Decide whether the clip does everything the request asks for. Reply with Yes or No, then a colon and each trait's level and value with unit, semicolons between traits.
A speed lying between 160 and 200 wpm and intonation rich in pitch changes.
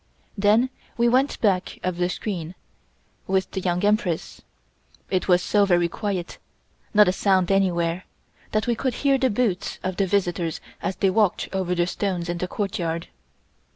No: average, 165 wpm; average, 2.8 semitones